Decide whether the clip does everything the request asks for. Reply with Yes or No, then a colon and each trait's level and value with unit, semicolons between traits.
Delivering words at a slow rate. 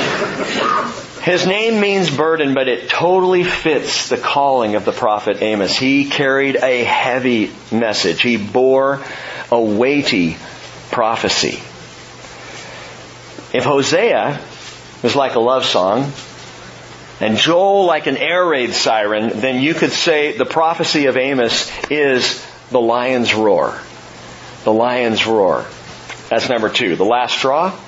Yes: slow, 125 wpm